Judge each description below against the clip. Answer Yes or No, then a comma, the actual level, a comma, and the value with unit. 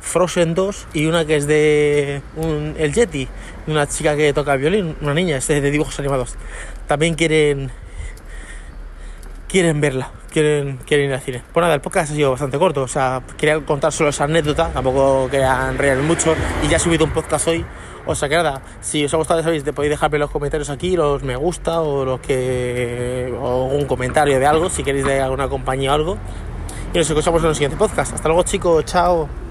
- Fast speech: Yes, fast, 200 wpm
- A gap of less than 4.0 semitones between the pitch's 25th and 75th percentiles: Yes, average, 3.1 semitones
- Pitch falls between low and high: Yes, medium, 150 Hz